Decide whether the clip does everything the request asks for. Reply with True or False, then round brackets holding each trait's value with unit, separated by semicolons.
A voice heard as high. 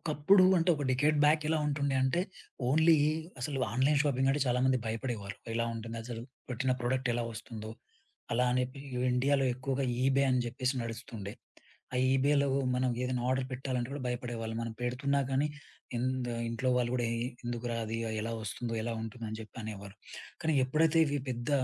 False (125 Hz)